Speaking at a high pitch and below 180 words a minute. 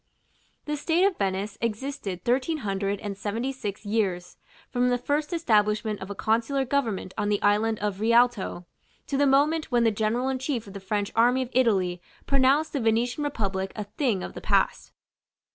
No: high, 225 Hz; average, 185 wpm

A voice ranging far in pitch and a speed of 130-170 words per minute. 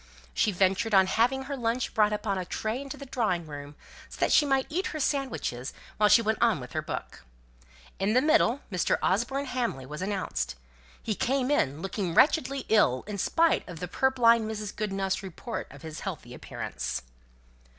No: wide, 6.0 semitones; average, 180 wpm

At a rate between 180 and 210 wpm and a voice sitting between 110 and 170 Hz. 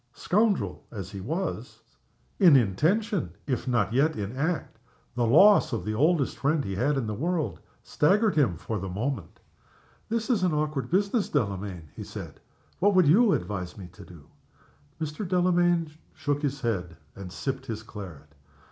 No: average, 165 wpm; medium, 140 Hz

